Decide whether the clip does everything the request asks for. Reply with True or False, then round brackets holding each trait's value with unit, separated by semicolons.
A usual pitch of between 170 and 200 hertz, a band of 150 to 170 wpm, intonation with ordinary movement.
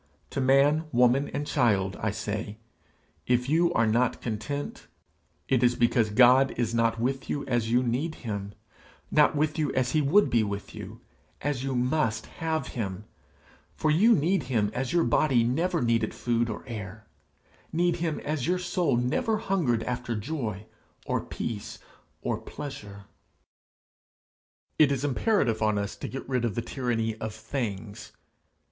False (125 Hz; 160 wpm; 4.6 semitones)